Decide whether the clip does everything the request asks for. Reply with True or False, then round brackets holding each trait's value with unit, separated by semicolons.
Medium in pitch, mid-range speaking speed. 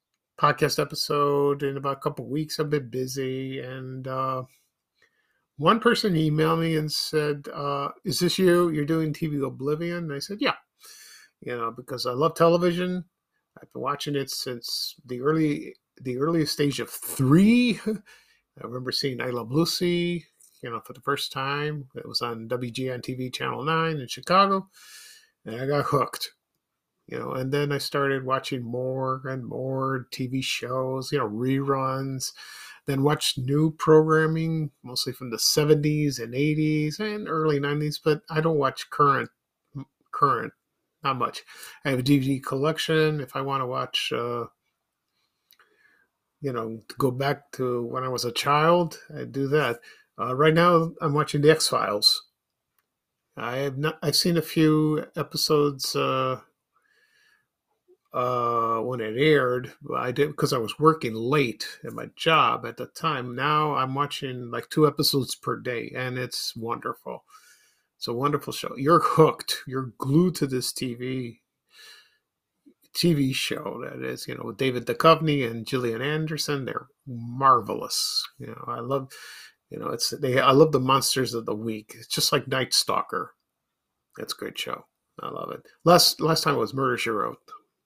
True (145 Hz; 165 wpm)